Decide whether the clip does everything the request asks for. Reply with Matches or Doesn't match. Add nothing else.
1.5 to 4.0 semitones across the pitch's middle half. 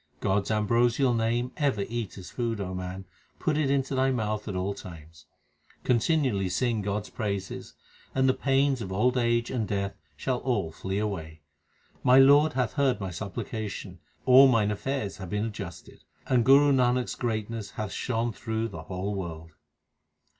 Doesn't match